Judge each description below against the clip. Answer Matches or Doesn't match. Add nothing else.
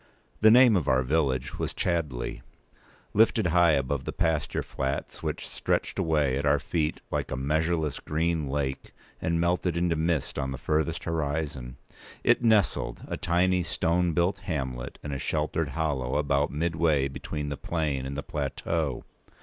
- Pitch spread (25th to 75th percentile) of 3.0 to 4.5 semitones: Matches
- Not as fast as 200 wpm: Matches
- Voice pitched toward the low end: Matches